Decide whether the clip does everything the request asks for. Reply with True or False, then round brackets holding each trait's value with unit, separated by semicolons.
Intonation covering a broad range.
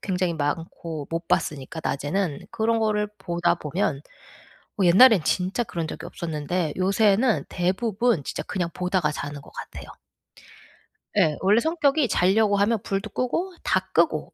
False (4.9 semitones)